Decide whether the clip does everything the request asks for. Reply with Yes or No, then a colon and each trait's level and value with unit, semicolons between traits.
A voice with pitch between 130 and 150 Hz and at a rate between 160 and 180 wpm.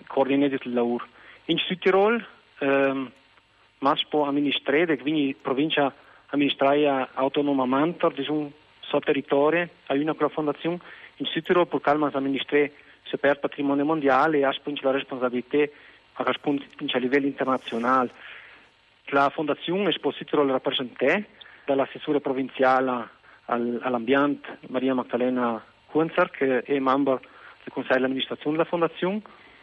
No: medium, 140 Hz; average, 125 wpm